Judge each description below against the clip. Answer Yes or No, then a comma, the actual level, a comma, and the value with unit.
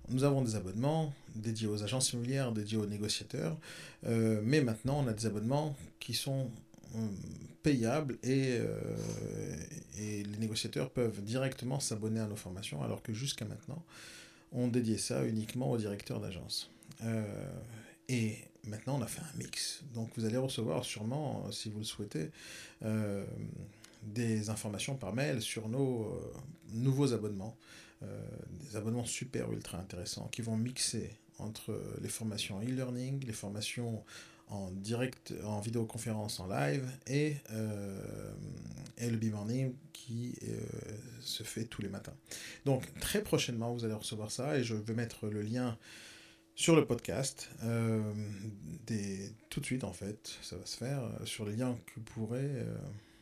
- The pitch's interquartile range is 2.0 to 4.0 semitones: Yes, average, 3.5 semitones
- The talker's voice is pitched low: Yes, low, 115 Hz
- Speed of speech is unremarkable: Yes, average, 155 wpm